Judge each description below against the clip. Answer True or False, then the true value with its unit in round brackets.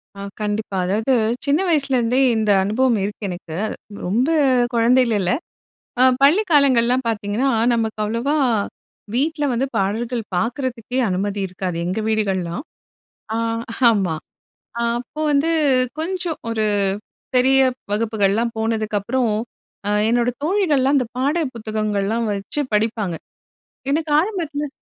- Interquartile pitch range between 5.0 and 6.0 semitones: False (4.6 semitones)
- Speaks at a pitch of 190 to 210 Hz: False (230 Hz)